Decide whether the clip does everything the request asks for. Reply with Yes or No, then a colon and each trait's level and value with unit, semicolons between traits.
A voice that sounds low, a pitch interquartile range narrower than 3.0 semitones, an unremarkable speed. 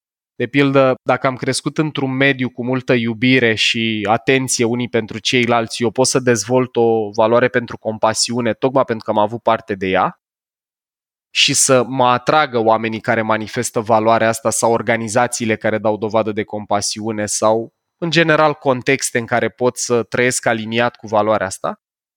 Yes: low, 120 Hz; narrow, 2.4 semitones; average, 160 wpm